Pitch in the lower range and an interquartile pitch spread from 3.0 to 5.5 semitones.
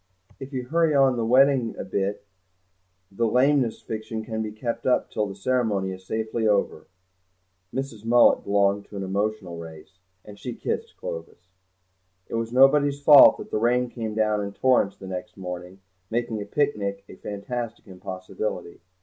Yes: low, 110 Hz; average, 4.0 semitones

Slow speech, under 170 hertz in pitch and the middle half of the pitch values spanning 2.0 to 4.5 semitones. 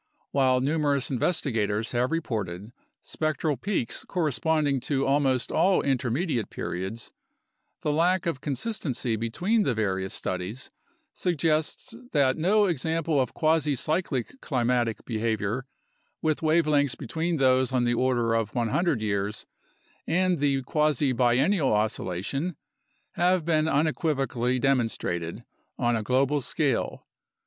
No: slow, 120 wpm; low, 135 Hz; average, 5.1 semitones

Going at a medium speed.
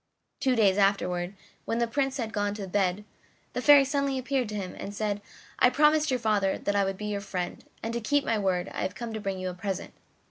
No: fast, 240 wpm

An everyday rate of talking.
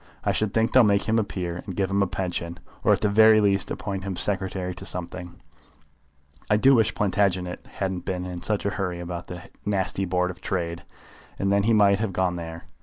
No: fast, 215 wpm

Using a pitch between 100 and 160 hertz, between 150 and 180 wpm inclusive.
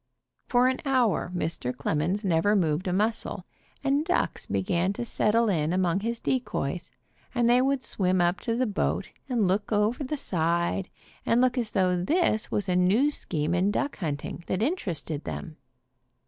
No: high, 200 Hz; average, 175 wpm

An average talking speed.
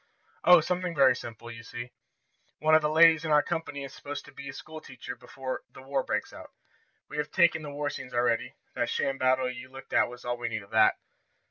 No: fast, 230 wpm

